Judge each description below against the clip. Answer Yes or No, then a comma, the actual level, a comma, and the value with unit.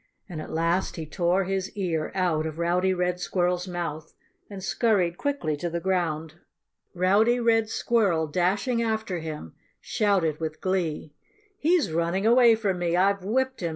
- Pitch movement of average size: Yes, average, 3.5 semitones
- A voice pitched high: No, medium, 180 Hz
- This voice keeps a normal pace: Yes, average, 155 wpm